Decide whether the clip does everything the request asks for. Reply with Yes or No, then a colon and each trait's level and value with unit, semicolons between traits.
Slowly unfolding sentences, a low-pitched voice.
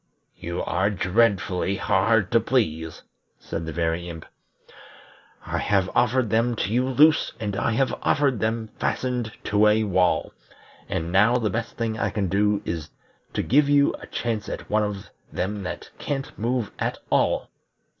No: average, 165 wpm; low, 105 Hz